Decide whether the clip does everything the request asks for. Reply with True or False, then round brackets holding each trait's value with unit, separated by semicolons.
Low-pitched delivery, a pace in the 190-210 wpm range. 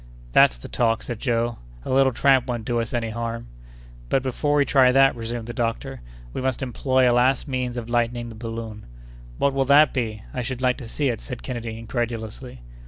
True (120 Hz; 205 wpm)